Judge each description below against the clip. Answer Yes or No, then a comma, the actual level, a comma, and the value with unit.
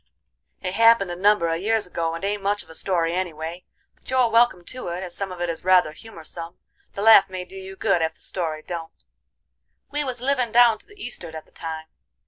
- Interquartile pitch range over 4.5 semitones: Yes, average, 4.9 semitones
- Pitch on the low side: No, medium, 185 Hz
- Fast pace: Yes, fast, 230 wpm